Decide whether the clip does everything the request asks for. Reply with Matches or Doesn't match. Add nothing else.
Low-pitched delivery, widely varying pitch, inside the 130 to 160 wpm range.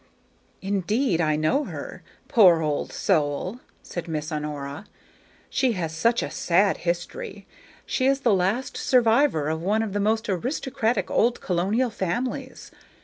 Doesn't match